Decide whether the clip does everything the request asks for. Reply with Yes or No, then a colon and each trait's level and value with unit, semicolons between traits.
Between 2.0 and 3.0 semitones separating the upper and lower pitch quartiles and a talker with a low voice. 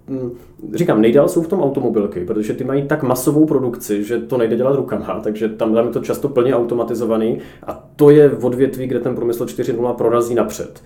Yes: narrow, 2.4 semitones; low, 120 Hz